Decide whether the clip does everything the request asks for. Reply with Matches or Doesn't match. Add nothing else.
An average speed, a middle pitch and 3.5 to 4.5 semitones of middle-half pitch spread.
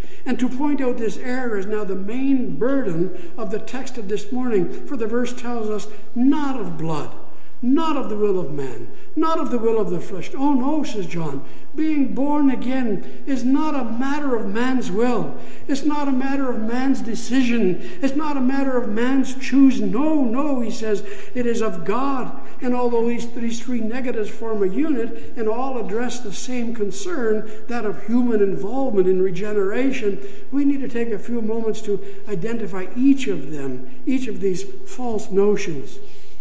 Doesn't match